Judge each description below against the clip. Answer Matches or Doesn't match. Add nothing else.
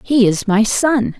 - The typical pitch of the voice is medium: Doesn't match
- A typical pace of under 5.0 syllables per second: Matches